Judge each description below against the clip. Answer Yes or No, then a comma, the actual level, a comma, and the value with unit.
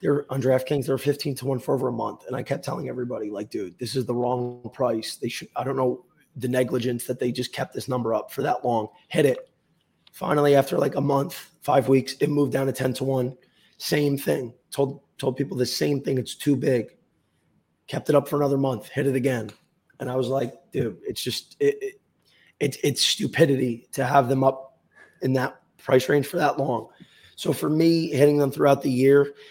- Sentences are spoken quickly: Yes, fast, 220 wpm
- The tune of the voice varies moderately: No, narrow, 2.0 semitones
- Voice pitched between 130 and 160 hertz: Yes, low, 135 Hz